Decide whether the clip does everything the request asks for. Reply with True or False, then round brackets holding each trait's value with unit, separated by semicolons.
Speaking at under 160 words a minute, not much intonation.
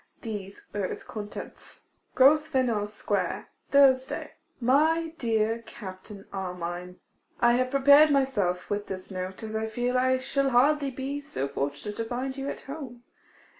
False (145 wpm; 5.0 semitones)